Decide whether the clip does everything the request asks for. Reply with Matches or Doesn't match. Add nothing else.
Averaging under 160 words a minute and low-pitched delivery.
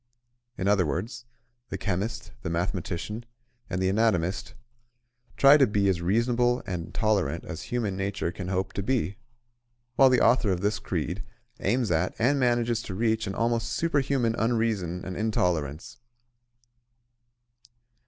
Matches